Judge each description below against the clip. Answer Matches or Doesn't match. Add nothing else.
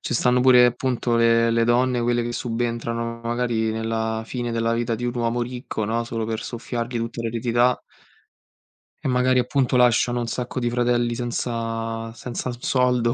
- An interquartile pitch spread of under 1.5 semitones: Matches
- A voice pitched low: Matches